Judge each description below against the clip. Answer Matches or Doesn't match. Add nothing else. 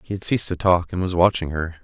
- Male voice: Matches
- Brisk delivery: Matches